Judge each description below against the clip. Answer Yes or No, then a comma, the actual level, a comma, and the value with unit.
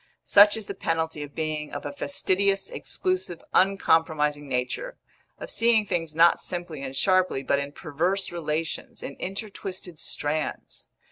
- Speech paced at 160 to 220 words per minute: No, average, 140 wpm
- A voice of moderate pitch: Yes, medium, 165 Hz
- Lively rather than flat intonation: No, average, 4.6 semitones